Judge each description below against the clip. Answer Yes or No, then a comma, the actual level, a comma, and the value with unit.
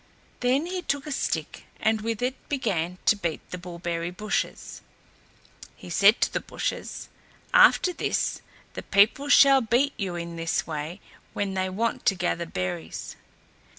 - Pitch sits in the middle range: No, high, 200 Hz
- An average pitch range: No, wide, 6.5 semitones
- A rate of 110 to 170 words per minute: Yes, average, 150 wpm